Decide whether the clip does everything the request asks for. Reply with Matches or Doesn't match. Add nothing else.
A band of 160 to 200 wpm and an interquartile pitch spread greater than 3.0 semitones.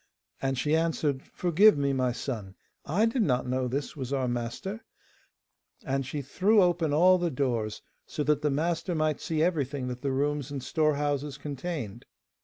Matches